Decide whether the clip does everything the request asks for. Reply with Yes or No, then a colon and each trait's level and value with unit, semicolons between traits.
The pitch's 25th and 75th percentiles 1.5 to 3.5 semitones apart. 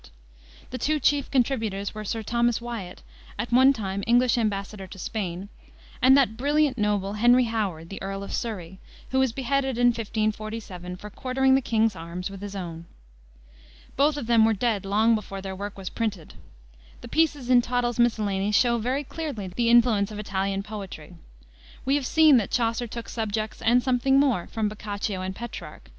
No: average, 3.9 semitones